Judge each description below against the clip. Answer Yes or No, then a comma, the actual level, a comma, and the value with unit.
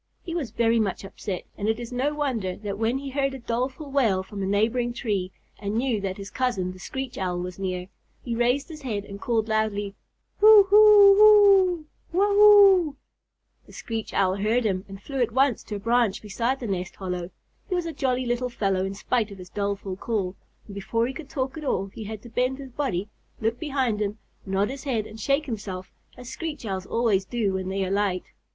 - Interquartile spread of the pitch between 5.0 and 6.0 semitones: Yes, average, 5.3 semitones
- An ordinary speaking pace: No, fast, 210 wpm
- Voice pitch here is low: No, high, 230 Hz